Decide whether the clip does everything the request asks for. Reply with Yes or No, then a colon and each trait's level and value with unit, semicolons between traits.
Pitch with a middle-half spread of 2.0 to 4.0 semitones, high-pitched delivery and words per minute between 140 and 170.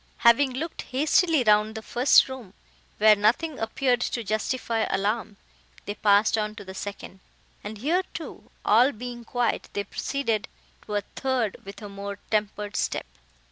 Yes: average, 3.5 semitones; high, 220 Hz; average, 155 wpm